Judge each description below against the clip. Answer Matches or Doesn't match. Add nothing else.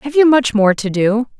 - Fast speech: Matches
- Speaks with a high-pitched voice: Matches